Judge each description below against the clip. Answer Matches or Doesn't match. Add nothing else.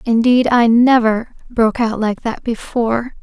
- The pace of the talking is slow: Matches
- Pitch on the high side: Matches